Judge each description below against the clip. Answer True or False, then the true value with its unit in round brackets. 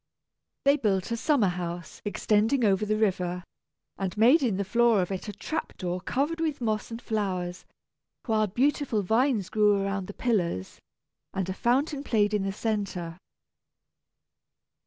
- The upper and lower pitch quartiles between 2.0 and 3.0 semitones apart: False (4.0 semitones)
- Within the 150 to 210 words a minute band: True (155 wpm)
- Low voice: False (210 Hz)